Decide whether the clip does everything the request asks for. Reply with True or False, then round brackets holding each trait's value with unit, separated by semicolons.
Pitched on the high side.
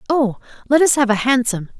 True (250 Hz)